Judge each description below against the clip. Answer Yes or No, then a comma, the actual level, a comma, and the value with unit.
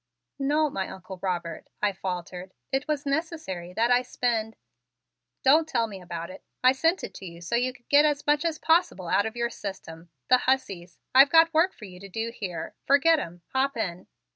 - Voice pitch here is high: Yes, high, 235 Hz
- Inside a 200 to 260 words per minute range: Yes, fast, 205 wpm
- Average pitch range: No, wide, 7.6 semitones